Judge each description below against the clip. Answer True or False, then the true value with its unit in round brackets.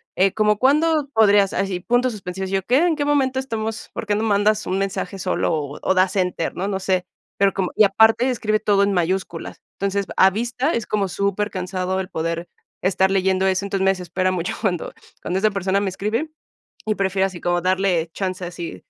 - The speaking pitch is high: True (195 Hz)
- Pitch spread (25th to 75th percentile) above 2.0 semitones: True (2.5 semitones)